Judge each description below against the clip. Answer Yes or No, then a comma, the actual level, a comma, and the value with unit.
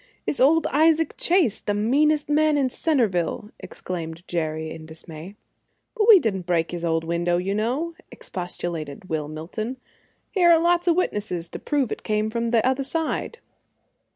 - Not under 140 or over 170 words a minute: Yes, average, 160 wpm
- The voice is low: No, high, 215 Hz